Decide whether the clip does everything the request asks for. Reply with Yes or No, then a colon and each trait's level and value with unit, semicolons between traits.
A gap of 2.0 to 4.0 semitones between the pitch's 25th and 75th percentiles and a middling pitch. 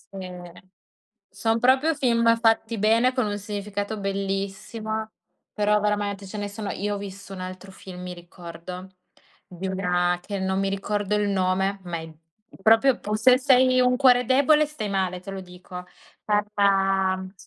No: average, 2.9 semitones; high, 200 Hz